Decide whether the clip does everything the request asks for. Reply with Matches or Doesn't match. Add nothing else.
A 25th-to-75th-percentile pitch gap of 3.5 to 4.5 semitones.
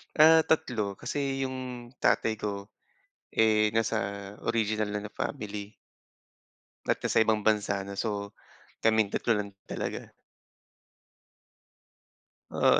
Doesn't match